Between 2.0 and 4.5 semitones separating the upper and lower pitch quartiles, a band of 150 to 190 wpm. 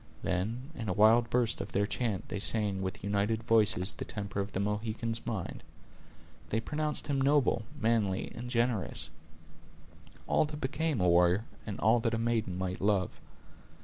Yes: average, 3.0 semitones; average, 165 wpm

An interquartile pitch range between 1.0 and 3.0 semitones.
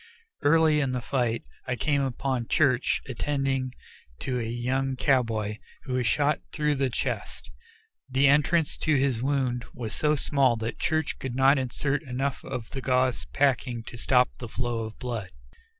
Yes: narrow, 2.6 semitones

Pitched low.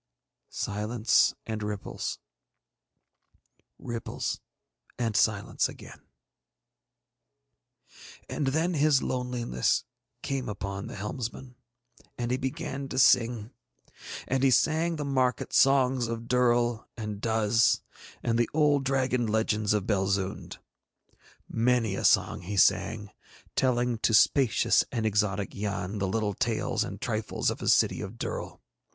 Yes: low, 115 Hz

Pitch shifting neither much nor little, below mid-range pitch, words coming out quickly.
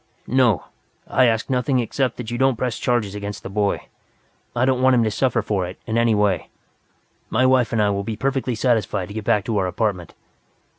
Yes: average, 3.5 semitones; low, 115 Hz; fast, 210 wpm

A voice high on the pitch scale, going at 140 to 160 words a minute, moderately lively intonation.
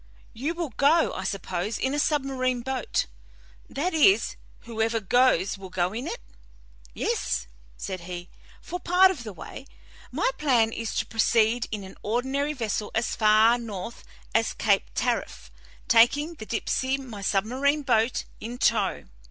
Yes: high, 235 Hz; average, 150 wpm; average, 4.3 semitones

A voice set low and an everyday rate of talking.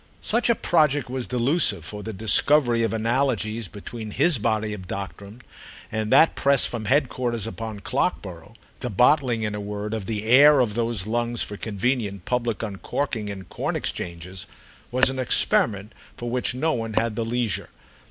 Yes: low, 115 Hz; average, 160 wpm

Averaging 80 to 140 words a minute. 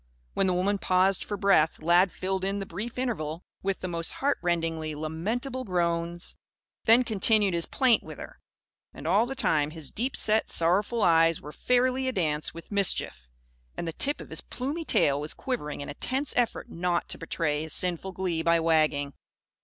No: average, 185 wpm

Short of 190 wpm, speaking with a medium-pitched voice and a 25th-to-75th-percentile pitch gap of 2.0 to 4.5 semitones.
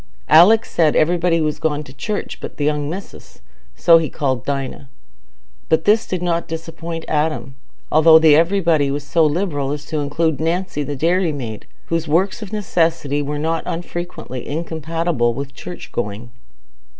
Yes: average, 150 wpm; medium, 160 Hz; average, 2.8 semitones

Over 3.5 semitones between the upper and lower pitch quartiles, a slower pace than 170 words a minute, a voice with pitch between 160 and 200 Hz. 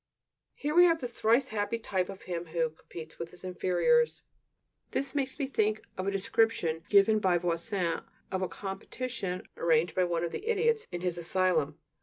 No: wide, 5.5 semitones; average, 180 wpm; high, 190 Hz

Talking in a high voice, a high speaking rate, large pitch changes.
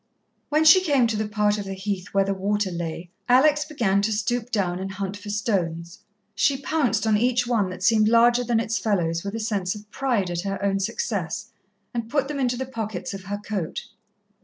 No: high, 210 Hz; fast, 210 wpm; average, 3.8 semitones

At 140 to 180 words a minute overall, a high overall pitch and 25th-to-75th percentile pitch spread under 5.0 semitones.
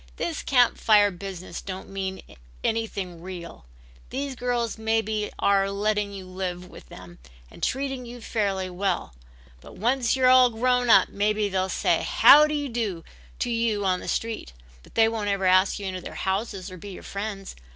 Yes: average, 170 wpm; high, 205 Hz; average, 3.7 semitones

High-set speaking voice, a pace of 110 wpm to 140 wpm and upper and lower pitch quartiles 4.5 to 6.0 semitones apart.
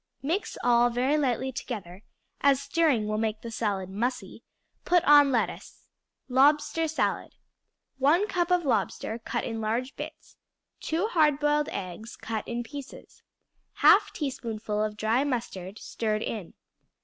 Yes: high, 245 Hz; slow, 135 wpm; average, 5.2 semitones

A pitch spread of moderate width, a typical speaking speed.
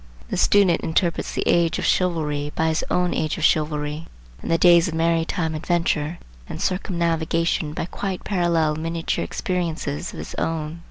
No: narrow, 1.7 semitones; average, 160 wpm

